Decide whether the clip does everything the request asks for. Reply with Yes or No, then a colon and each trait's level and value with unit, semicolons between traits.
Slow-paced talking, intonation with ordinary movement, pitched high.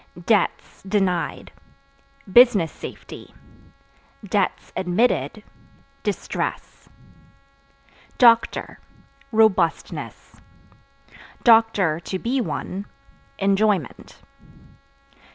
Yes: slow, 45 wpm; average, 3.9 semitones; high, 200 Hz